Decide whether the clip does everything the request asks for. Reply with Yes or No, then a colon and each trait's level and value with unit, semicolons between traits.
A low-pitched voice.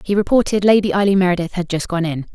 No: medium, 185 Hz